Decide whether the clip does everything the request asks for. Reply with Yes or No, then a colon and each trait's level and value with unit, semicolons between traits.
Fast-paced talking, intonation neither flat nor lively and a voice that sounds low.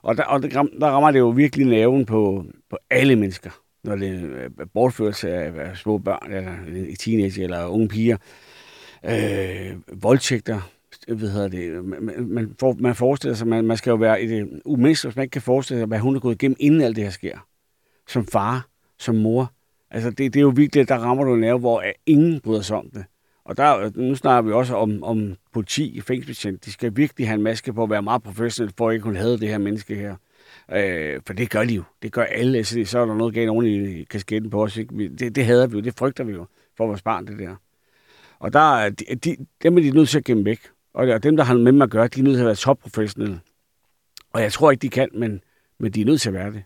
Yes: fast, 245 wpm; average, 3.6 semitones; low, 115 Hz